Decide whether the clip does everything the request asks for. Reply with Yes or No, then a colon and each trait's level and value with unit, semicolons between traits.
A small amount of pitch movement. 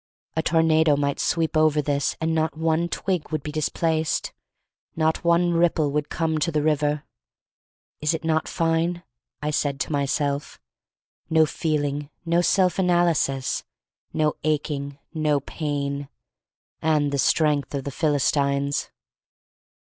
Yes: narrow, 2.1 semitones